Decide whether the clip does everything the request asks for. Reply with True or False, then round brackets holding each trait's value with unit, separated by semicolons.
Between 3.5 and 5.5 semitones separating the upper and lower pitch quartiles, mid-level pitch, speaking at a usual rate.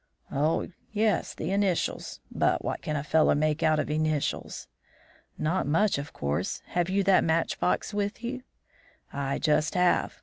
True (4.3 semitones; 160 Hz; 155 wpm)